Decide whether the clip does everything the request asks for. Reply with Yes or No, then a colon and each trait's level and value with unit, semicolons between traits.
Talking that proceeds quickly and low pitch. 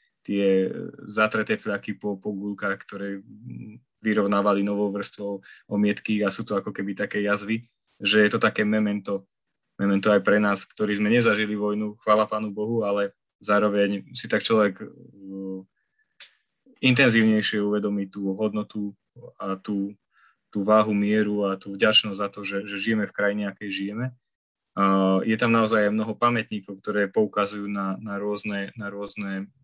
No: average, 145 wpm; low, 105 Hz